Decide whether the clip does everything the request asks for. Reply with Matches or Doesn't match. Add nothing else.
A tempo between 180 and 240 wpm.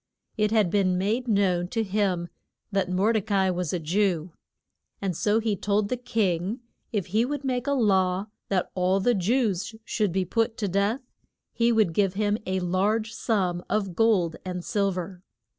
Matches